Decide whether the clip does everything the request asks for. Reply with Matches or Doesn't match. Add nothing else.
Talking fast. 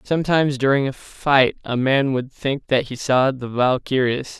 Doesn't match